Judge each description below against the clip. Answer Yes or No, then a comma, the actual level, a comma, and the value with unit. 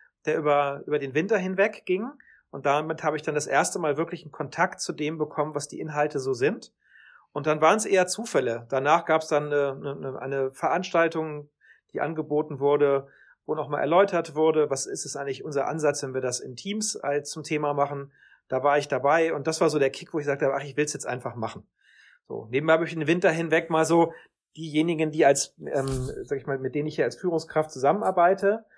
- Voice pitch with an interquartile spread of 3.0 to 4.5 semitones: No, narrow, 2.6 semitones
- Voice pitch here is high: No, medium, 155 Hz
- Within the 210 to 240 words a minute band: Yes, fast, 215 wpm